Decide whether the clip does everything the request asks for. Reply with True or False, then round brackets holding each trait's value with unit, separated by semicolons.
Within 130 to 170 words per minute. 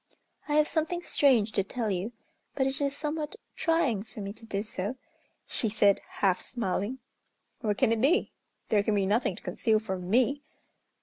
False (180 wpm)